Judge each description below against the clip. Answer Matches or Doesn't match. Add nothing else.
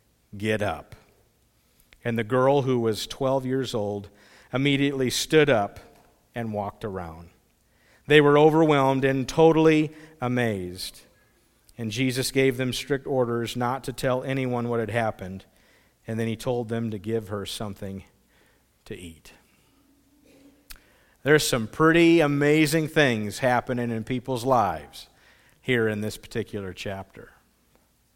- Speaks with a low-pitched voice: Matches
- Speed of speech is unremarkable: Doesn't match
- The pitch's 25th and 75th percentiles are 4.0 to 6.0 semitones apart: Matches